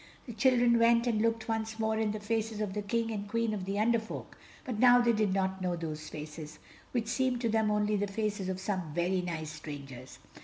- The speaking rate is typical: No, fast, 225 wpm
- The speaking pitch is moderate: No, high, 210 Hz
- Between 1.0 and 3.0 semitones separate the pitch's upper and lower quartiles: No, average, 3.5 semitones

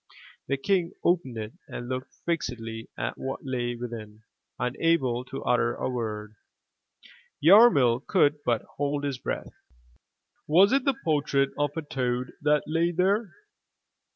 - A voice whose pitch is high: No, low, 135 Hz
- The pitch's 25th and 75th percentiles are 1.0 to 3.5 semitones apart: No, average, 5.3 semitones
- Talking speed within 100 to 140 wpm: Yes, slow, 135 wpm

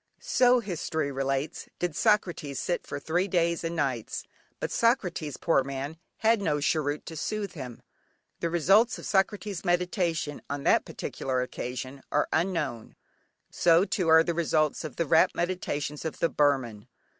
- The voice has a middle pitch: Yes, medium, 160 Hz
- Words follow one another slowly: No, average, 155 wpm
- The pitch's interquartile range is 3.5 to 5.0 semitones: Yes, average, 4.1 semitones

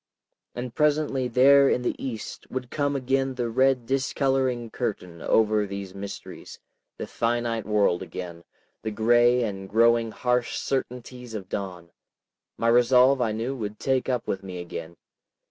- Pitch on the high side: No, low, 120 Hz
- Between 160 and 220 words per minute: No, average, 145 wpm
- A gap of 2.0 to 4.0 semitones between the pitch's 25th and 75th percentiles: Yes, average, 3.7 semitones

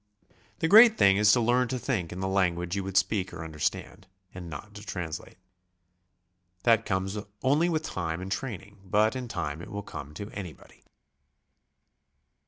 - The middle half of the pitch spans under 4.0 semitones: No, average, 4.4 semitones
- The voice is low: Yes, low, 100 Hz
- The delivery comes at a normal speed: Yes, average, 170 wpm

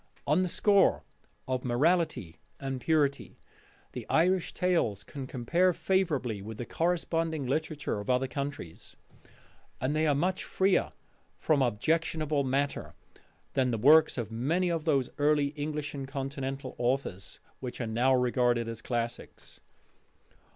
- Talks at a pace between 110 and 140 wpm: Yes, slow, 135 wpm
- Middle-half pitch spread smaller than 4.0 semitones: No, average, 4.3 semitones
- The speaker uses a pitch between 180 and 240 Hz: No, medium, 140 Hz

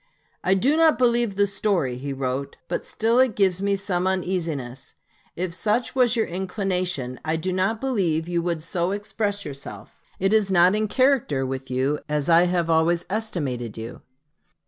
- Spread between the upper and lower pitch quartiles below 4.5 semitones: No, wide, 5.5 semitones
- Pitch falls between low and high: Yes, medium, 180 Hz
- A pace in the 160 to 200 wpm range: Yes, average, 170 wpm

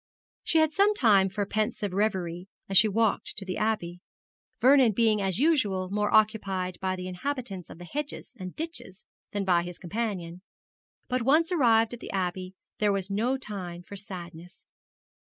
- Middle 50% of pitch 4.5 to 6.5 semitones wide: No, average, 4.0 semitones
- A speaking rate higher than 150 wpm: Yes, average, 170 wpm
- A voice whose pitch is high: Yes, high, 200 Hz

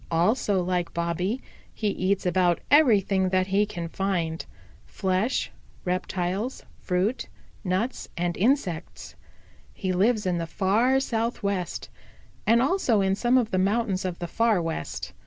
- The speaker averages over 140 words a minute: No, slow, 135 wpm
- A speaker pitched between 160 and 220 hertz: Yes, high, 190 Hz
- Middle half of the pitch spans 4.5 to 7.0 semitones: No, average, 3.9 semitones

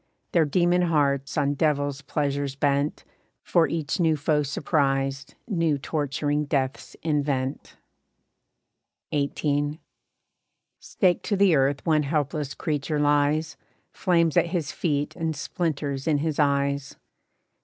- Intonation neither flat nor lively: No, narrow, 2.2 semitones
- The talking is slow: Yes, slow, 115 wpm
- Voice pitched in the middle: Yes, medium, 145 Hz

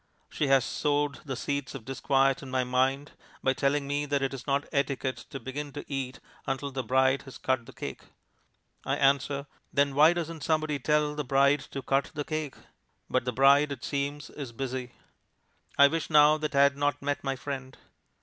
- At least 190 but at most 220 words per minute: Yes, average, 195 wpm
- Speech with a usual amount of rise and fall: No, narrow, 1.6 semitones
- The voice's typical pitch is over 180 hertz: No, medium, 140 Hz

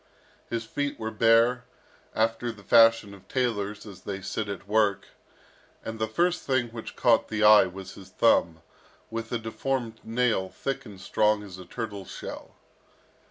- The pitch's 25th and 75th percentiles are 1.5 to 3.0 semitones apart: Yes, narrow, 2.5 semitones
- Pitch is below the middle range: Yes, low, 110 Hz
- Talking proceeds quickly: No, average, 160 wpm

